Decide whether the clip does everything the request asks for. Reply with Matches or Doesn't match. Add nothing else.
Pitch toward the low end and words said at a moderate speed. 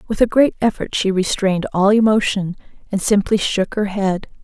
Doesn't match